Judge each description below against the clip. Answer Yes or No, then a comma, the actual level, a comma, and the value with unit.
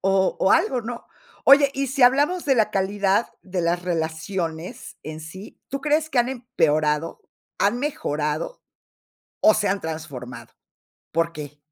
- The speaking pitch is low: No, high, 195 Hz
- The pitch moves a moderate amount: No, wide, 7.8 semitones